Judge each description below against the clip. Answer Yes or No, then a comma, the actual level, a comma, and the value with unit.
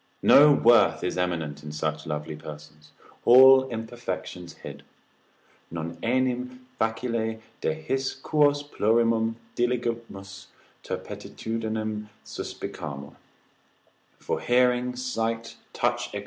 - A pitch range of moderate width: No, wide, 5.9 semitones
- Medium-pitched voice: No, low, 115 Hz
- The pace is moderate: No, slow, 95 wpm